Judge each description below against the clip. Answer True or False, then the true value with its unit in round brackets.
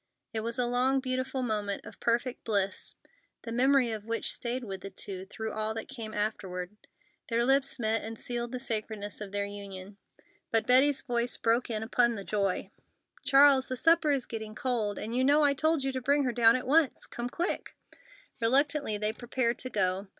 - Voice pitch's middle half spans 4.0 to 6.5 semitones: False (3.4 semitones)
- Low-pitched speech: False (235 Hz)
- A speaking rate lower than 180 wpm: False (195 wpm)